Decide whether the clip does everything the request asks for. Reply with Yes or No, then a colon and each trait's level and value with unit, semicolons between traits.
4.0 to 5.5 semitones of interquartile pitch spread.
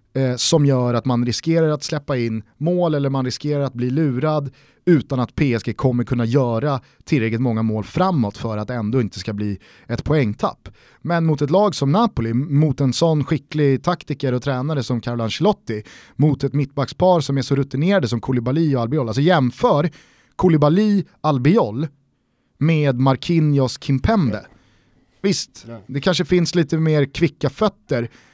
Yes: average, 4.4 semitones